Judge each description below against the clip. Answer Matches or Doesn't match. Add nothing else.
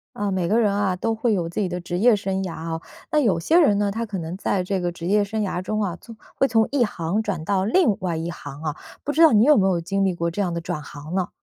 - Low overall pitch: Doesn't match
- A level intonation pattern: Doesn't match